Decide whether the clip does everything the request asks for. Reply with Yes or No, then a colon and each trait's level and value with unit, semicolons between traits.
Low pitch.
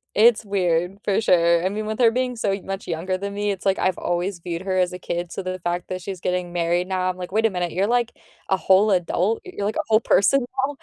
No: high, 190 Hz